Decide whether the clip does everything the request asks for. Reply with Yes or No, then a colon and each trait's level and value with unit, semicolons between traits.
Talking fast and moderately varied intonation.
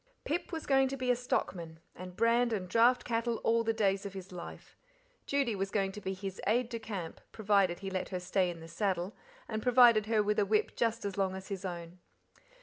Yes: fast, 225 wpm; average, 3.6 semitones